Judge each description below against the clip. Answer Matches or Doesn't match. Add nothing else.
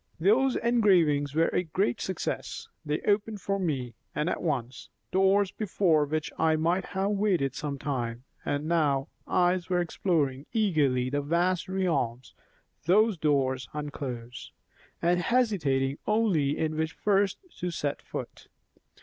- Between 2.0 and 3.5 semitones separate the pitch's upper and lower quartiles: Doesn't match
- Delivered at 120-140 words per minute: Matches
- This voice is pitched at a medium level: Matches